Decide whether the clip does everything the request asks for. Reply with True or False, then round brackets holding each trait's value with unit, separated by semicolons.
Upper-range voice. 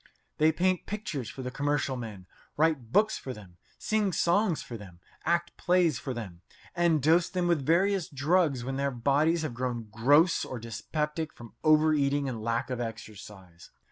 False (140 Hz)